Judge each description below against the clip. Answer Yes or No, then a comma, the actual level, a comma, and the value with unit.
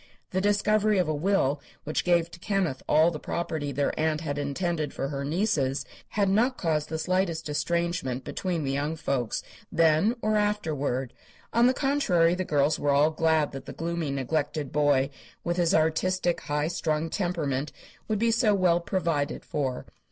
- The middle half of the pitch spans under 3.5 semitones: No, average, 4.1 semitones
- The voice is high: No, medium, 160 Hz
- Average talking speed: Yes, average, 170 wpm